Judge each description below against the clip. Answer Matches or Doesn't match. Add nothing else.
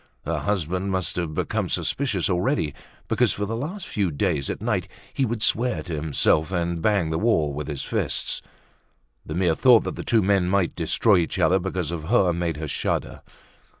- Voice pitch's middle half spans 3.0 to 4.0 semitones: Doesn't match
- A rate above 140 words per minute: Matches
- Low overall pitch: Matches